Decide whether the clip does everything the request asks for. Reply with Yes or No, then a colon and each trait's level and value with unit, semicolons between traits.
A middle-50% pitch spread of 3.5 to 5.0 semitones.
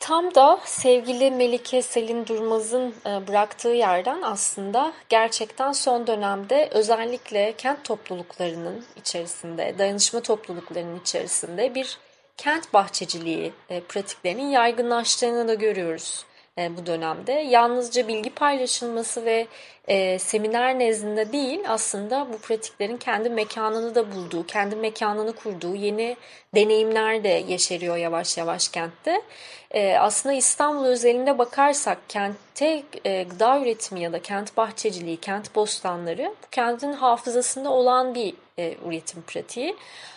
Yes: average, 4.1 semitones